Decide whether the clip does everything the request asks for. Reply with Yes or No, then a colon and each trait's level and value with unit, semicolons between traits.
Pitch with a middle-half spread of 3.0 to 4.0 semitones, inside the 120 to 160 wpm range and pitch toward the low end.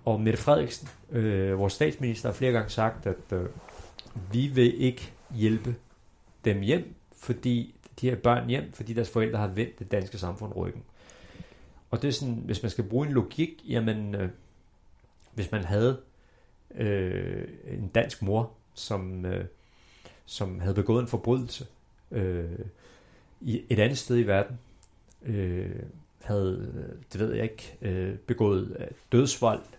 Yes: average, 3.5 semitones; average, 150 wpm; low, 115 Hz